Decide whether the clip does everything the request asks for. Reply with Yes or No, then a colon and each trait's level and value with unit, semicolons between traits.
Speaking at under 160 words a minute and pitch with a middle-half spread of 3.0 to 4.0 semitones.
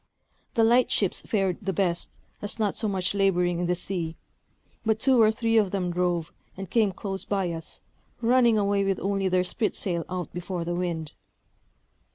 No: average, 180 wpm; average, 3.3 semitones